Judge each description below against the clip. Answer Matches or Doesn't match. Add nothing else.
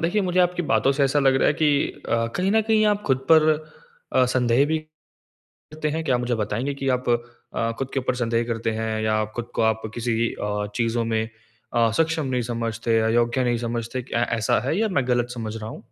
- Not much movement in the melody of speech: Doesn't match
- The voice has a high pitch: Doesn't match